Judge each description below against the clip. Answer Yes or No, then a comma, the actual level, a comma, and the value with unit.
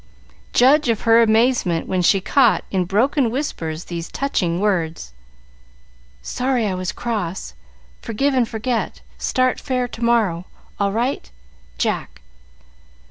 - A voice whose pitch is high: Yes, high, 220 Hz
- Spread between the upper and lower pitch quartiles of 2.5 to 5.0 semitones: No, wide, 5.6 semitones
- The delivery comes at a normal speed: No, slow, 125 wpm